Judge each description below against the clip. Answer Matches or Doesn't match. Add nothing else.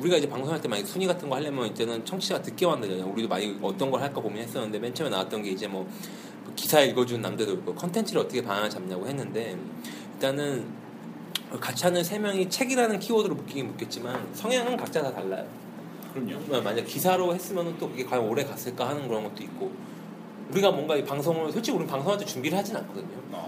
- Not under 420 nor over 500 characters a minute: Matches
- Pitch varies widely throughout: Matches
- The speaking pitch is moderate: Matches